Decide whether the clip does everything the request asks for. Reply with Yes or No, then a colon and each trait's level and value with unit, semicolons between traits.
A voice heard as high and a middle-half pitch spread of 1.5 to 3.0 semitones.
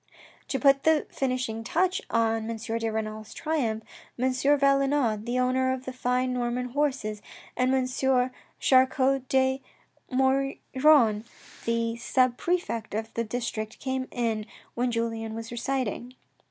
Yes: very high, 250 Hz; narrow, 2.6 semitones